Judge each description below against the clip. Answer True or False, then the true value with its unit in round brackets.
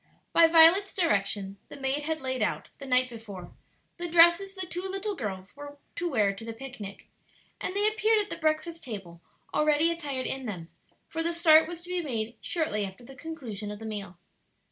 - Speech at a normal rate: True (195 wpm)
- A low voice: False (285 Hz)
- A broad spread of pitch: True (7.8 semitones)